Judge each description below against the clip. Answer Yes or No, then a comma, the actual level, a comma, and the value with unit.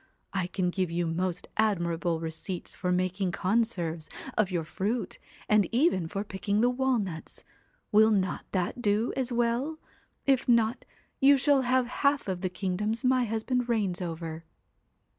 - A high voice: Yes, high, 205 Hz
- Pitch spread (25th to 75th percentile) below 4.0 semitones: No, average, 5.1 semitones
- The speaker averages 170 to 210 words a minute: No, average, 150 wpm